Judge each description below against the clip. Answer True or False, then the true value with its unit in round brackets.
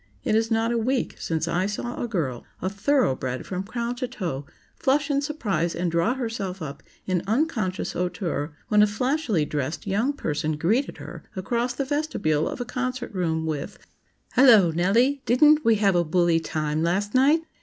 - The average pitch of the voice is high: True (205 Hz)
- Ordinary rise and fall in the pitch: False (6.9 semitones)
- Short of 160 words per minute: False (175 wpm)